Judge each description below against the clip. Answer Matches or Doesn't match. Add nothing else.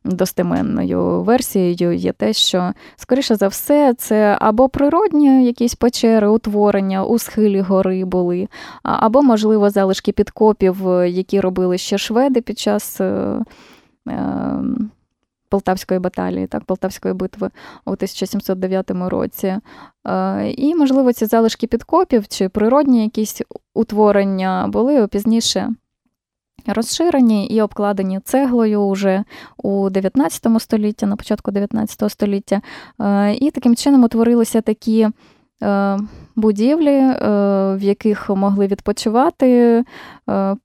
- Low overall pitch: Doesn't match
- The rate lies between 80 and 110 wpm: Matches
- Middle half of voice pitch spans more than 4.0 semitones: Doesn't match